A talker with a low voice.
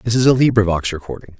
Yes: low, 100 Hz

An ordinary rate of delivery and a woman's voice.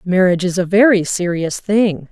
Yes: average, 170 wpm; female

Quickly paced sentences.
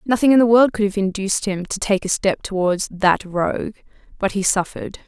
Yes: fast, 215 wpm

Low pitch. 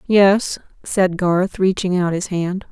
No: medium, 185 Hz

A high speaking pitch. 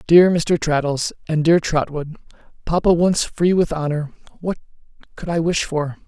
No: medium, 160 Hz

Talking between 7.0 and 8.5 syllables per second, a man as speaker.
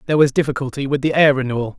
Yes: 8.0 syllables/s; male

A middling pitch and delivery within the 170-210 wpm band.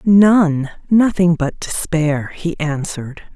No: medium, 165 Hz; slow, 90 wpm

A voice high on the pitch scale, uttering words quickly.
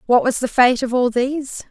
Yes: very high, 255 Hz; fast, 245 wpm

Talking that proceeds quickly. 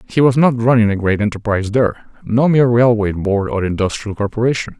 No: average, 190 wpm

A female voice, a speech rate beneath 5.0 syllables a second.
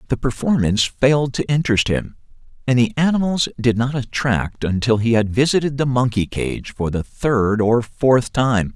No: male; 4.8 syllables/s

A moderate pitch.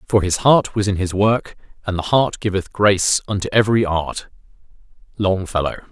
No: low, 100 Hz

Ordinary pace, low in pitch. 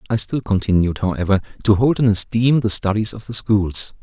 Yes: average, 195 wpm; low, 105 Hz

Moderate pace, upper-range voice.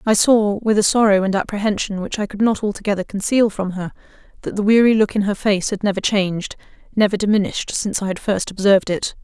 No: fast, 215 wpm; high, 205 Hz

